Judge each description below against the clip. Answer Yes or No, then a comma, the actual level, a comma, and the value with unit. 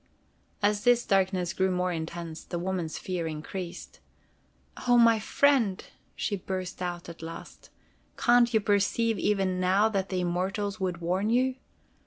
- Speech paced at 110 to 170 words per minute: Yes, average, 145 wpm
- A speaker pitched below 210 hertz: Yes, high, 190 Hz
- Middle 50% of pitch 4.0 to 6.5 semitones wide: No, average, 3.2 semitones